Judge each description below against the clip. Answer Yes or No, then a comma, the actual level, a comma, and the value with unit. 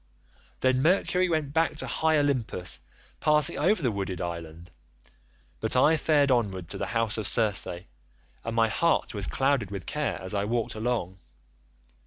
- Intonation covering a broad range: Yes, wide, 7.3 semitones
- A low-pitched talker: Yes, low, 115 Hz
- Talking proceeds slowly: No, average, 160 wpm